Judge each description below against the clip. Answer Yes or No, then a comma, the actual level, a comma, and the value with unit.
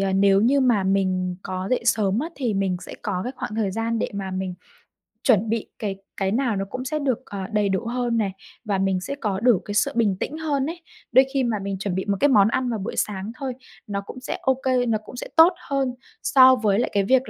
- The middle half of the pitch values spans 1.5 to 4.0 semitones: No, average, 4.6 semitones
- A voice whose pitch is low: No, high, 215 Hz